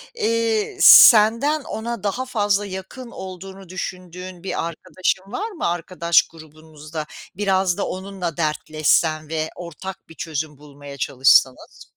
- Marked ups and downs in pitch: No, average, 4.6 semitones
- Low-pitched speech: No, medium, 185 Hz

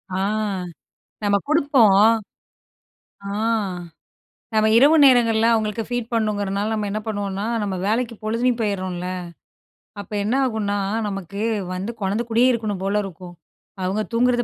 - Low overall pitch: No, high, 215 Hz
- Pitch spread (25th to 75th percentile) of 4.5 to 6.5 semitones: No, average, 2.8 semitones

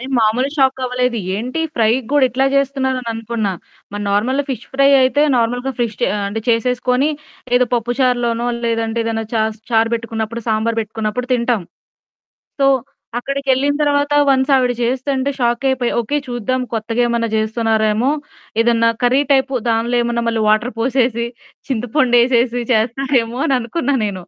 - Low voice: No, high, 240 Hz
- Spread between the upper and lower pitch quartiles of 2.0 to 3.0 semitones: Yes, narrow, 2.5 semitones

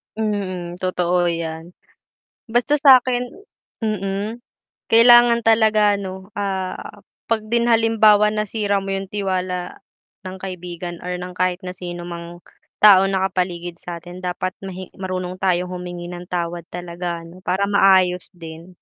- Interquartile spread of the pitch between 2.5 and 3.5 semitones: Yes, average, 2.9 semitones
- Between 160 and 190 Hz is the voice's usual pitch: Yes, medium, 185 Hz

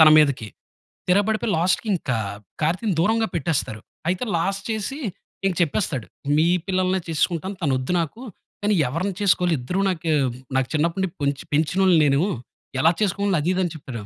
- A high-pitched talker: No, medium, 175 Hz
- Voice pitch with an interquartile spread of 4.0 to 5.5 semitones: Yes, average, 4.3 semitones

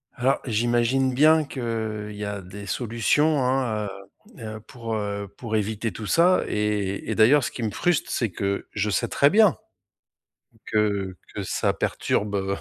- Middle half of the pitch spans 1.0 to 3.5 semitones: No, average, 3.9 semitones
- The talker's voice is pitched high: No, low, 110 Hz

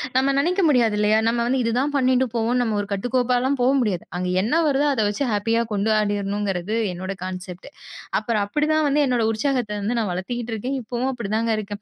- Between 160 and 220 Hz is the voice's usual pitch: No, high, 230 Hz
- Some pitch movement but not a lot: Yes, average, 3.8 semitones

